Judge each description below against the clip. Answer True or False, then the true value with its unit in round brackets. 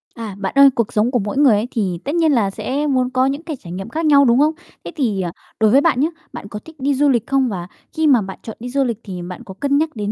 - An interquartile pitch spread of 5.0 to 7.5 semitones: True (5.3 semitones)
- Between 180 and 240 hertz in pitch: False (250 Hz)